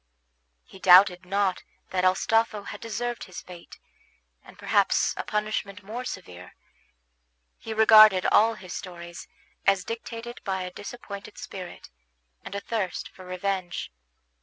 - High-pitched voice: Yes, high, 195 Hz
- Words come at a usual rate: No, slow, 130 wpm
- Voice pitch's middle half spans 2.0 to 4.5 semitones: Yes, average, 3.0 semitones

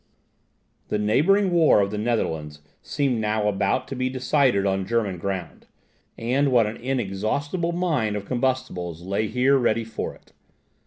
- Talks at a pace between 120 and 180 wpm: Yes, average, 150 wpm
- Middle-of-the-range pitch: No, low, 115 Hz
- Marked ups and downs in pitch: No, average, 4.9 semitones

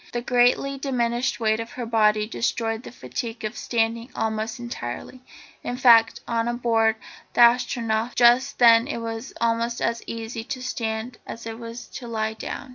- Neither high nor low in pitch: No, high, 230 Hz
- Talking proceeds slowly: No, average, 165 wpm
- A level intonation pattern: Yes, narrow, 1.3 semitones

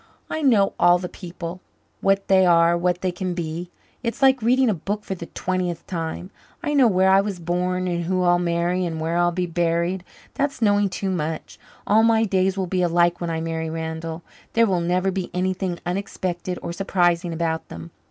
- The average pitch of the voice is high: No, medium, 180 Hz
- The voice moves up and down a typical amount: No, narrow, 2.1 semitones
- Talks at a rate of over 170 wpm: Yes, average, 200 wpm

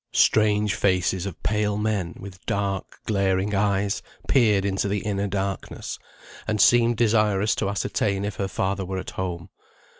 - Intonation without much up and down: Yes, narrow, 1.5 semitones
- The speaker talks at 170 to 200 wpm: No, average, 150 wpm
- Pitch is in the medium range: No, low, 100 Hz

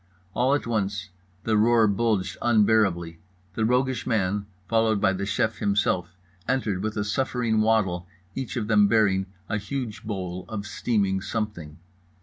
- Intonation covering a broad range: No, narrow, 2.6 semitones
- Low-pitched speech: Yes, low, 105 Hz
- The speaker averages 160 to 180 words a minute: No, average, 145 wpm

